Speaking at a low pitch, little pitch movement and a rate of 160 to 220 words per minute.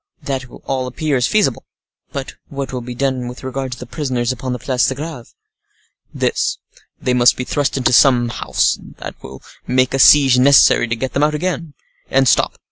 Yes: low, 130 Hz; narrow, 1.9 semitones; average, 185 wpm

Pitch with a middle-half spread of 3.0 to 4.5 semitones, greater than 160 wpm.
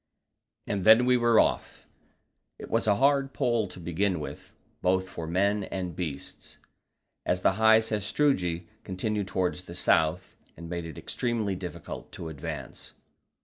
No: average, 4.1 semitones; average, 145 wpm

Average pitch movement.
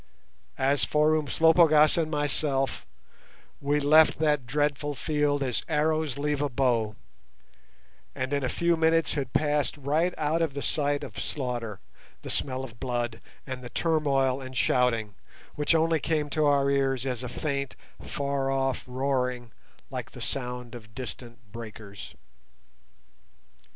Yes: average, 3.1 semitones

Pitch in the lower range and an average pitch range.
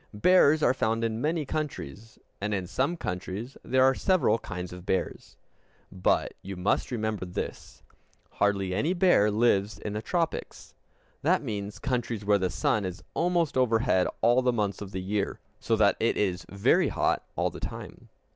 Yes: low, 105 Hz; average, 4.9 semitones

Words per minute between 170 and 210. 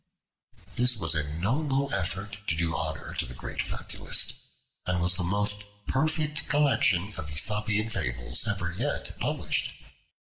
No: average, 140 wpm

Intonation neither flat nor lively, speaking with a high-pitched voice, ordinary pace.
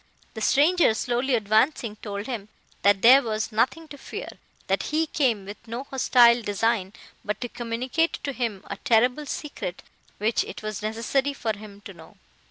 Yes: average, 3.9 semitones; high, 230 Hz; average, 170 wpm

